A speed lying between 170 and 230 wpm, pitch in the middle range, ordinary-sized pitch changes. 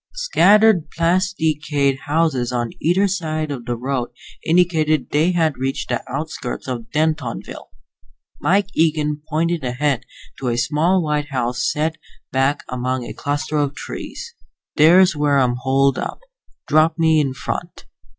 No: average, 140 wpm; medium, 150 Hz; average, 3.8 semitones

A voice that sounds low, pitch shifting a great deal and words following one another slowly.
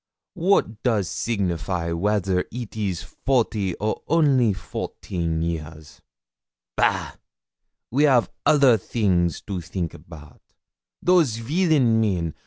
Yes: low, 105 Hz; wide, 6.4 semitones; slow, 105 wpm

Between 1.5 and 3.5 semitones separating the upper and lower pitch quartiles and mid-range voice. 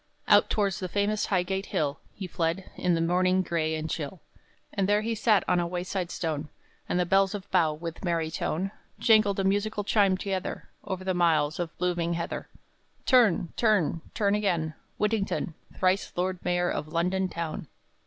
Yes: average, 2.8 semitones; medium, 180 Hz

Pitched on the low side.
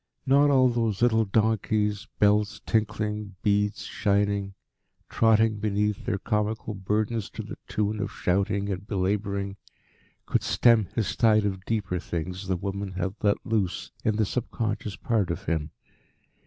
Yes: low, 105 Hz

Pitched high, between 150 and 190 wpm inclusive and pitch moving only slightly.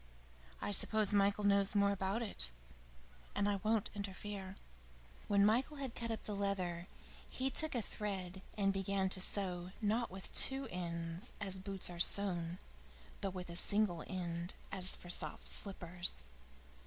Yes: high, 195 Hz; average, 155 wpm; narrow, 2.3 semitones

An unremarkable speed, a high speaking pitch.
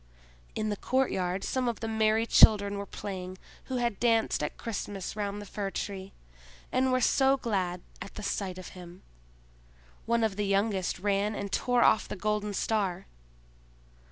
Yes: average, 165 wpm; high, 205 Hz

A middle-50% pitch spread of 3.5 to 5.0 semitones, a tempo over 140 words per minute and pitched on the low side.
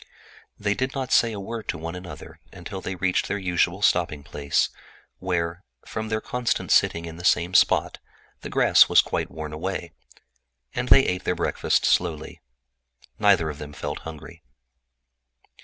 Yes: average, 3.9 semitones; average, 155 wpm; very low, 90 Hz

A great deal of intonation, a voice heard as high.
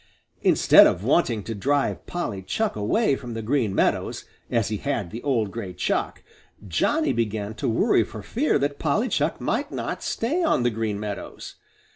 No: wide, 5.7 semitones; low, 115 Hz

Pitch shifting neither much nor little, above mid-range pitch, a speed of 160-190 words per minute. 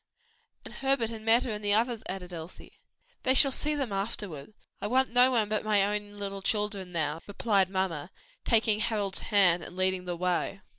Yes: average, 3.3 semitones; high, 205 Hz; average, 185 wpm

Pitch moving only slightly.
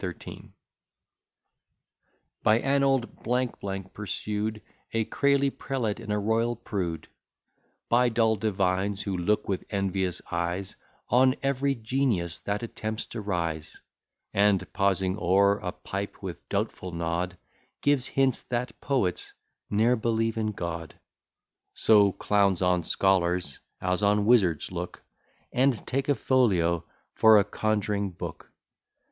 No: average, 4.2 semitones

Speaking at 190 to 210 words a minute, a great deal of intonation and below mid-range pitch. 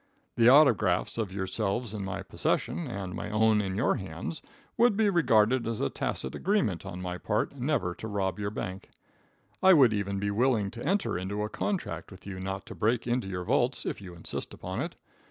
No: average, 200 wpm; average, 4.4 semitones; low, 105 Hz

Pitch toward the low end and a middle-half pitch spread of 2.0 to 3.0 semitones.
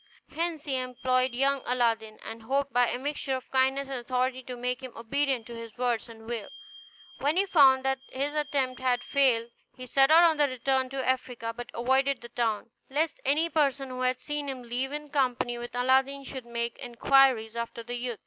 No: very high, 255 Hz; narrow, 2.4 semitones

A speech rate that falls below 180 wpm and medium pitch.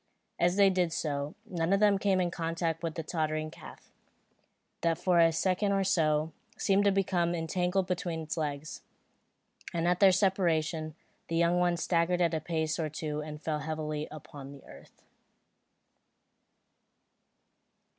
Yes: average, 150 wpm; medium, 165 Hz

